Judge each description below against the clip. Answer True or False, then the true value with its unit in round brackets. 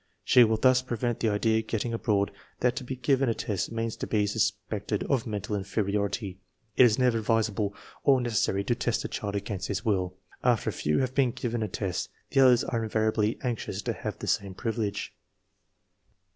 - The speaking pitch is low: True (110 Hz)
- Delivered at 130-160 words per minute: False (200 wpm)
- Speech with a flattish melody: False (3.0 semitones)